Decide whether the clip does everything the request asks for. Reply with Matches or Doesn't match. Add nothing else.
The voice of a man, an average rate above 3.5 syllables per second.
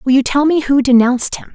Doesn't match